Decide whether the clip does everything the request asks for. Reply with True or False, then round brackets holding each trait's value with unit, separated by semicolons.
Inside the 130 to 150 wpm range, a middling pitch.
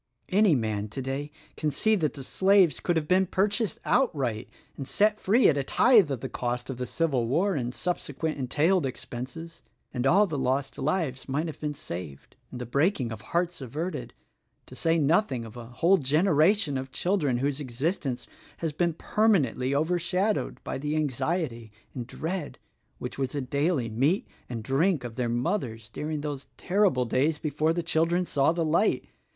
False (175 wpm; 150 Hz)